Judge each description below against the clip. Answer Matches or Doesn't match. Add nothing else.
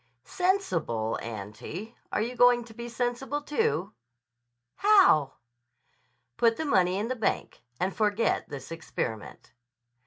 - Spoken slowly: Matches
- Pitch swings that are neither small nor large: Doesn't match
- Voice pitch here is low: Doesn't match